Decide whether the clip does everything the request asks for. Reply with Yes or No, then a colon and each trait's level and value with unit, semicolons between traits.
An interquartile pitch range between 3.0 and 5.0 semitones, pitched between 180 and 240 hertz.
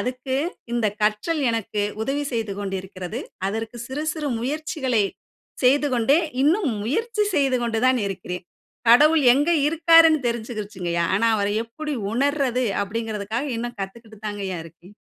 No: wide, 5.4 semitones; high, 235 Hz